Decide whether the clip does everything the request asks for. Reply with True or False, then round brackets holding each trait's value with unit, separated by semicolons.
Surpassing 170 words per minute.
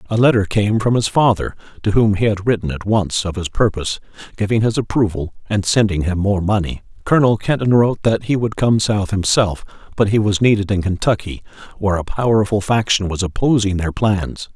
True (195 wpm)